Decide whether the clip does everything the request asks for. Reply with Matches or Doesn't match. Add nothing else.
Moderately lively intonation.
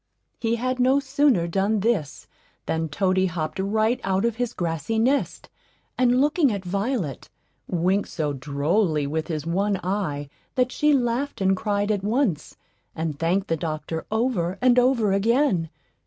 Doesn't match